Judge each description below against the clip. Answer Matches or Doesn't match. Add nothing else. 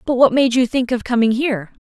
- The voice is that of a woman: Matches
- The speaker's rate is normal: Doesn't match